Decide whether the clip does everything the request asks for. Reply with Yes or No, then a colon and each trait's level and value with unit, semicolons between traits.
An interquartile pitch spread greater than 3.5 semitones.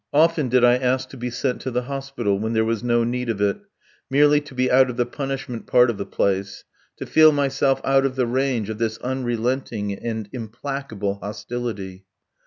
No: average, 3.2 semitones